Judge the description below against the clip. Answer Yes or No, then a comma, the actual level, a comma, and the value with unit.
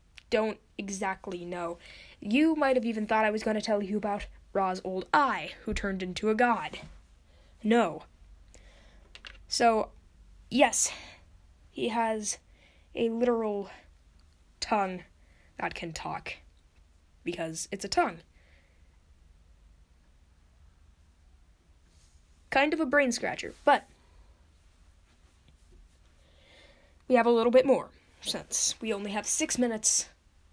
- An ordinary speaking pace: No, slow, 110 wpm